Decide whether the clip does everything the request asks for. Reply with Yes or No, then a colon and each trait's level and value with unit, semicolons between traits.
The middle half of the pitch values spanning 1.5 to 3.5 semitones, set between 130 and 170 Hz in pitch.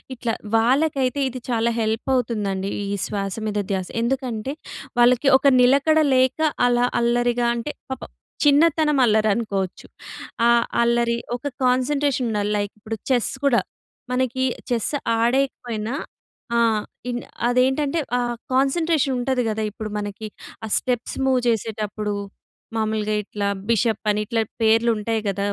No: average, 3.2 semitones; high, 240 Hz